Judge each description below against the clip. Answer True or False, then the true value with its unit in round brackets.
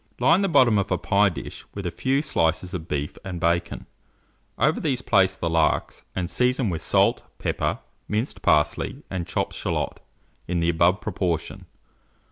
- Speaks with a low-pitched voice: True (95 Hz)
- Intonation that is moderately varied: False (5.8 semitones)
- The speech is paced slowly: False (165 wpm)